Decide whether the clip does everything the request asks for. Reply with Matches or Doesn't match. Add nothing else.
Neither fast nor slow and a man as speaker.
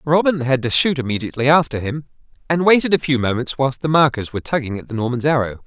Doesn't match